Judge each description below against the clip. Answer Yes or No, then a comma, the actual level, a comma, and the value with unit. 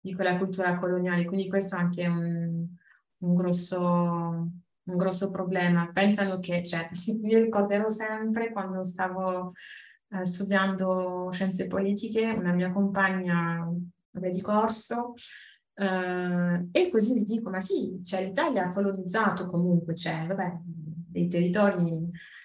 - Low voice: No, medium, 185 Hz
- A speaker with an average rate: Yes, average, 130 wpm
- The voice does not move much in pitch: Yes, narrow, 2.1 semitones